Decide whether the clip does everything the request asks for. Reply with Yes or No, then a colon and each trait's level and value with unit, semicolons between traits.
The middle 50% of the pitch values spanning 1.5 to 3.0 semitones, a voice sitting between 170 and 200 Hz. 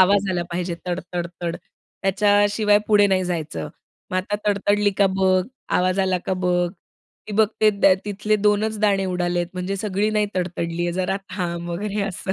Yes: narrow, 2.5 semitones; high, 190 Hz